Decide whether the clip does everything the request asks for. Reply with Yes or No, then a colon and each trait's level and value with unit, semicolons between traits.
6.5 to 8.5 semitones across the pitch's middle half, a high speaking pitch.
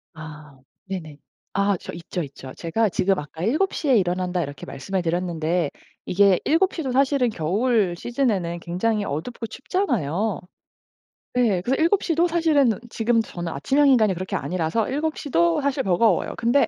Yes: wide, 7.1 semitones; high, 200 Hz